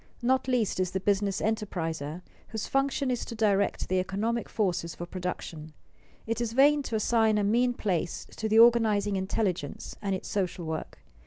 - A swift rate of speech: No, average, 170 wpm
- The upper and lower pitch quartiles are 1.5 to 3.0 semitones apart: No, average, 3.9 semitones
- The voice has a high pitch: Yes, high, 205 Hz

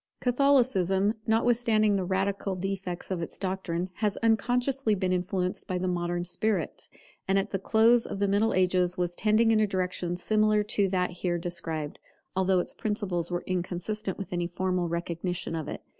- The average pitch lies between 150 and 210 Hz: Yes, high, 190 Hz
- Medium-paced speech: Yes, average, 170 wpm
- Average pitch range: Yes, average, 3.1 semitones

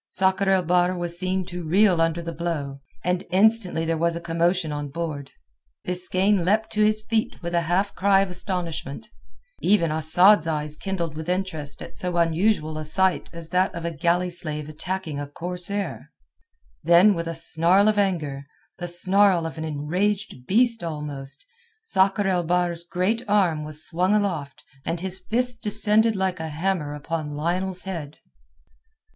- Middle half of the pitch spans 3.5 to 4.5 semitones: No, average, 3.1 semitones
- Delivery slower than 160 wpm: No, average, 165 wpm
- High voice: No, medium, 175 Hz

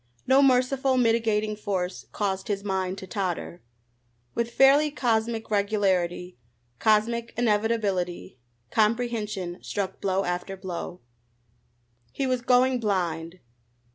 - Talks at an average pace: No, slow, 105 wpm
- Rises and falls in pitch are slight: No, average, 3.9 semitones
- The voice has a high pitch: Yes, high, 210 Hz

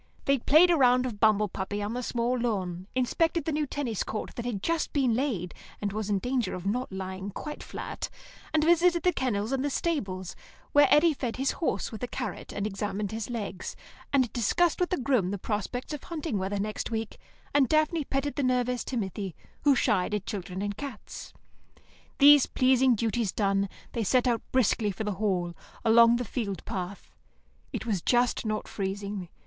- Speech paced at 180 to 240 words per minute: Yes, average, 190 wpm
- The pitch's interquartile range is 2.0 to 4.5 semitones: No, average, 5.0 semitones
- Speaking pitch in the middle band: No, high, 230 Hz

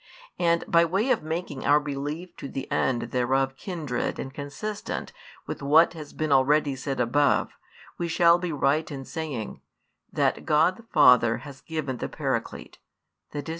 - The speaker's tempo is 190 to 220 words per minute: No, average, 160 wpm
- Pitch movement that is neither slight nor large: Yes, average, 3.7 semitones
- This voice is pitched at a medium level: Yes, medium, 145 Hz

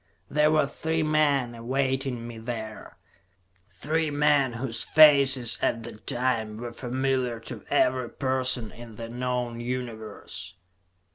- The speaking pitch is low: Yes, low, 125 Hz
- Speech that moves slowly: Yes, slow, 125 wpm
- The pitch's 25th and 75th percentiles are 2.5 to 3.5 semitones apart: Yes, average, 2.9 semitones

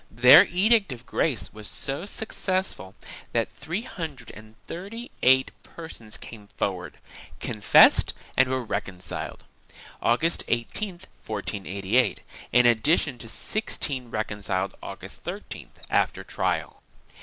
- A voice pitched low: Yes, low, 125 Hz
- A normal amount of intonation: No, wide, 7.5 semitones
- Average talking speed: No, slow, 115 wpm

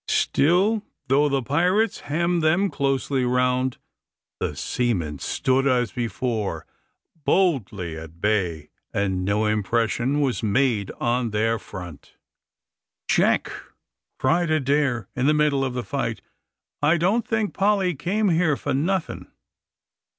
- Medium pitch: No, low, 130 Hz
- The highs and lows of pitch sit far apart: Yes, wide, 6.4 semitones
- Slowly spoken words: Yes, slow, 120 wpm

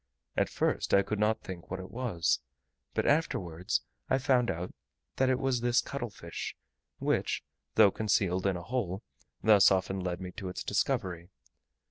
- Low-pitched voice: Yes, very low, 95 Hz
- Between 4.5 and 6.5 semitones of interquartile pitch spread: Yes, average, 4.9 semitones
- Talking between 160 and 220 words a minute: Yes, average, 165 wpm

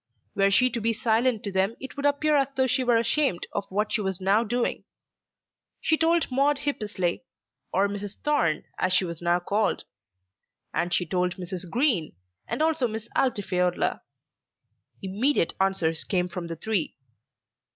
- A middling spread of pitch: No, wide, 5.9 semitones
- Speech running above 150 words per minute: Yes, average, 160 wpm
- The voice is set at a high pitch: Yes, high, 205 Hz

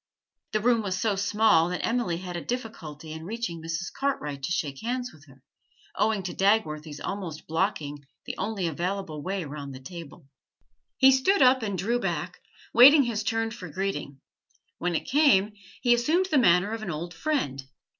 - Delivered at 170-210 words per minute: Yes, average, 175 wpm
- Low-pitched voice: No, high, 190 Hz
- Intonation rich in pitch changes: Yes, wide, 6.1 semitones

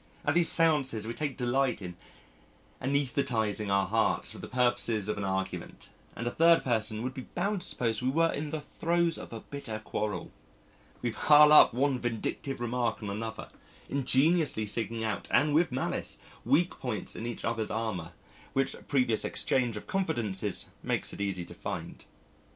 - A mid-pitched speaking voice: No, low, 120 Hz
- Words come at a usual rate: Yes, average, 170 wpm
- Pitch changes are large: No, average, 4.8 semitones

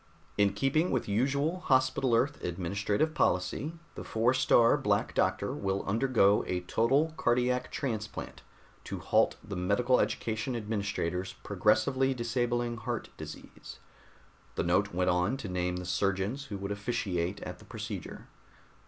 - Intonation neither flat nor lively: Yes, average, 5.0 semitones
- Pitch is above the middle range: No, low, 110 Hz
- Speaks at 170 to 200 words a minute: No, slow, 135 wpm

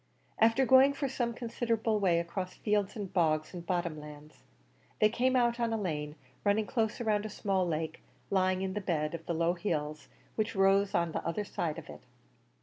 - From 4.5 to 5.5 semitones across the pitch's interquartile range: Yes, average, 4.8 semitones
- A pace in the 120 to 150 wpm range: No, average, 195 wpm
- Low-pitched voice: No, high, 195 Hz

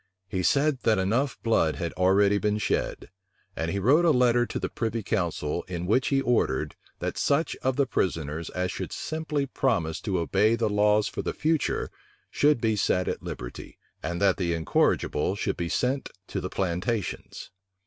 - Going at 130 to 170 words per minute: No, average, 180 wpm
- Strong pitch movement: Yes, wide, 6.0 semitones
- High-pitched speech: No, low, 105 Hz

